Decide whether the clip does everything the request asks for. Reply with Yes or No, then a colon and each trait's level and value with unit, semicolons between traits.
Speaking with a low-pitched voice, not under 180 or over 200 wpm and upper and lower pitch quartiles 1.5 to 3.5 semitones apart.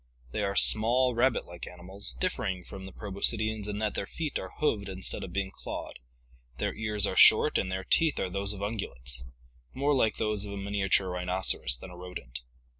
Yes: low, 100 Hz; average, 195 wpm; average, 2.9 semitones